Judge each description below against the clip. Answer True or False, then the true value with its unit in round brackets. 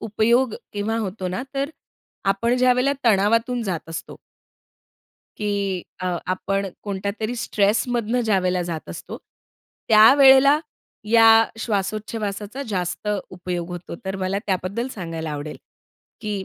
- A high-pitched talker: True (205 Hz)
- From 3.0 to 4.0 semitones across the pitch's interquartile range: True (3.7 semitones)